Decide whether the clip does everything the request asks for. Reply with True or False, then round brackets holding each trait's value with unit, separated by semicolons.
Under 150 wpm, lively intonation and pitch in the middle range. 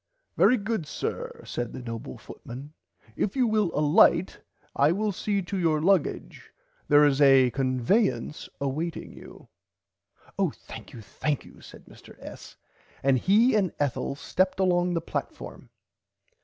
True (135 wpm; 6.3 semitones; 155 Hz)